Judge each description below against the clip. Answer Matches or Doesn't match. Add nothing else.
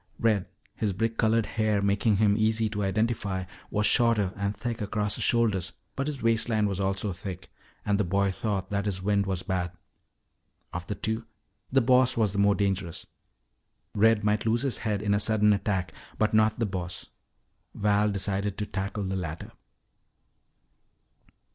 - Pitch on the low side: Matches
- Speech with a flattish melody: Matches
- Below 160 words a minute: Doesn't match